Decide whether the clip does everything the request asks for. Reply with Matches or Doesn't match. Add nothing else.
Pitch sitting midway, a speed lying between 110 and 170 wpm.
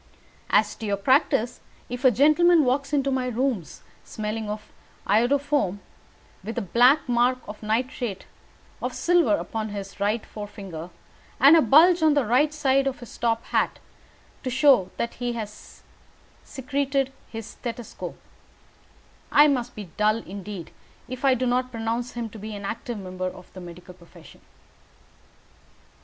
Doesn't match